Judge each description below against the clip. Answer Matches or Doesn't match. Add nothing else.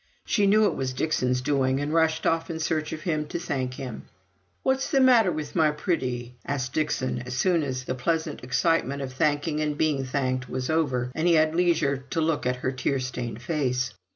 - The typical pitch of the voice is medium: Matches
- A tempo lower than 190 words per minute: Doesn't match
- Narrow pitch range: Doesn't match